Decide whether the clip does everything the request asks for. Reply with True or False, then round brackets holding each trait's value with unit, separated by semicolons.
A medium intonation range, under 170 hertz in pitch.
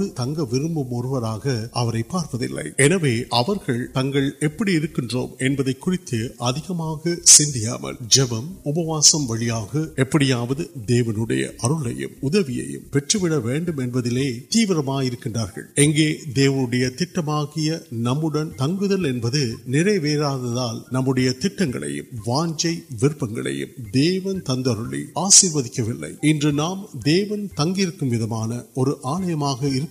True (4.6 semitones; 135 Hz)